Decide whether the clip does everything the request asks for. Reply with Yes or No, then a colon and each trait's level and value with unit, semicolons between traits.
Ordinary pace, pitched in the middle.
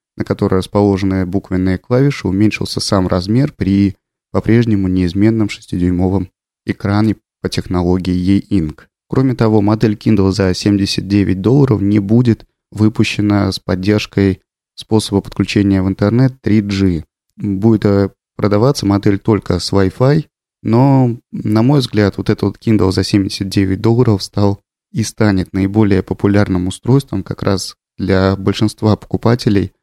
No: average, 120 wpm; low, 100 Hz